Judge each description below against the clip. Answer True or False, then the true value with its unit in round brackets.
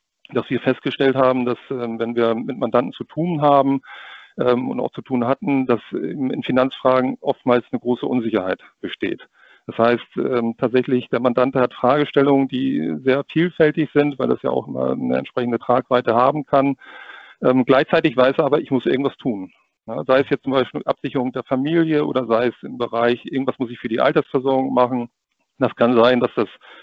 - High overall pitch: False (130 Hz)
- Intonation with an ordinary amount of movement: False (2.2 semitones)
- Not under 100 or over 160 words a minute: False (175 wpm)